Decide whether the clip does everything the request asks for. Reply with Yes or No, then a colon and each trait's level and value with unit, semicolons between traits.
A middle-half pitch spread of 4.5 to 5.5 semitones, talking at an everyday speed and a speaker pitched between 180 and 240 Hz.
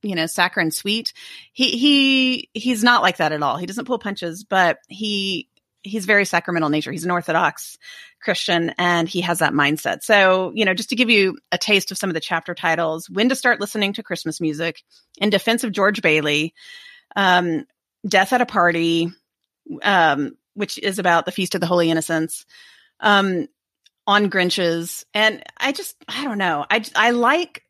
Yes: average, 4.8 semitones; average, 185 wpm; high, 190 Hz